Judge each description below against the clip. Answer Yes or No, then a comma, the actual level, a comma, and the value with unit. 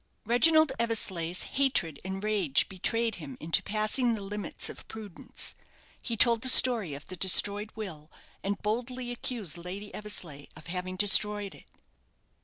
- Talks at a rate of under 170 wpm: Yes, average, 145 wpm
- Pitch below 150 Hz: No, high, 205 Hz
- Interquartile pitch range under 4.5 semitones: Yes, average, 4.1 semitones